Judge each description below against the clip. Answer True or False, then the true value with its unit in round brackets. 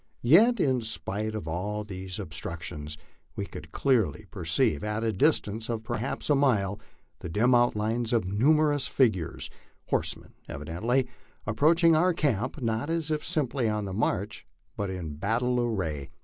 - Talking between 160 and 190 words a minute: False (150 wpm)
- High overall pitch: False (110 Hz)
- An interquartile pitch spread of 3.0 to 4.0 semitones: False (5.5 semitones)